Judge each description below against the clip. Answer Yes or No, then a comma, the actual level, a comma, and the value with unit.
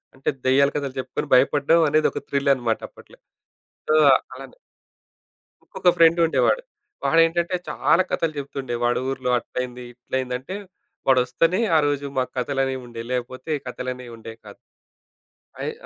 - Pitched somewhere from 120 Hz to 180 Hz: Yes, low, 135 Hz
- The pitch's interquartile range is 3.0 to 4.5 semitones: Yes, average, 3.5 semitones